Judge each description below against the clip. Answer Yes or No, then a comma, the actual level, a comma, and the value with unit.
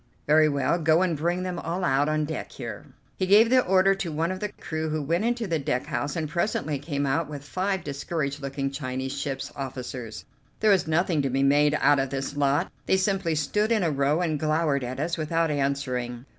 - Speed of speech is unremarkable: No, fast, 215 wpm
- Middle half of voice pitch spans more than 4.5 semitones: No, average, 3.9 semitones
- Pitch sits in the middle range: Yes, medium, 155 Hz